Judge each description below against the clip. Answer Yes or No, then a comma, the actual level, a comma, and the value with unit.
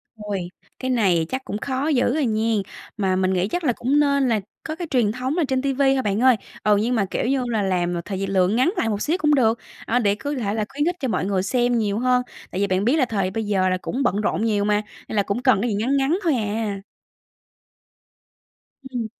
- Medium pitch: No, high, 225 Hz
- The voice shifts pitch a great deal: No, average, 4.5 semitones